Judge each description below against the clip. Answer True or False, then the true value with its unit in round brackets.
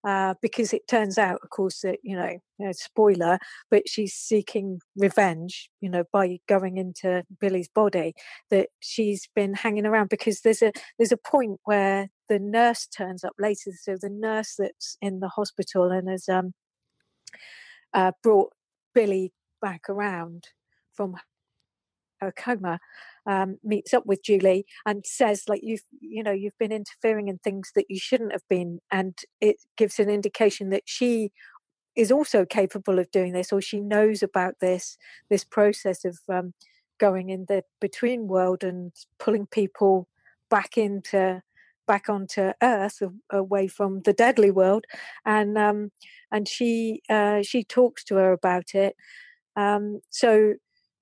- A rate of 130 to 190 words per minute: True (155 wpm)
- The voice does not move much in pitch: True (2.2 semitones)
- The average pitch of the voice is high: True (200 Hz)